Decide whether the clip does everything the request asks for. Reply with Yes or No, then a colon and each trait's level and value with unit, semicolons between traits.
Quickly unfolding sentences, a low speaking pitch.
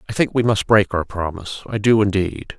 Yes: fast, 230 wpm; low, 100 Hz